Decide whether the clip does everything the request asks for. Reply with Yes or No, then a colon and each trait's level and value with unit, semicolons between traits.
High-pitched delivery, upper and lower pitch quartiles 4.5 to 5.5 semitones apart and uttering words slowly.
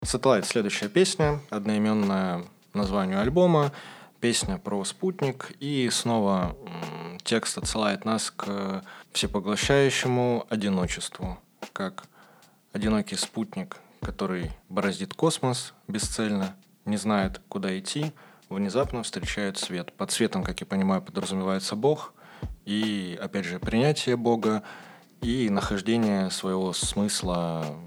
No: low, 105 Hz; average, 4.8 semitones; slow, 105 wpm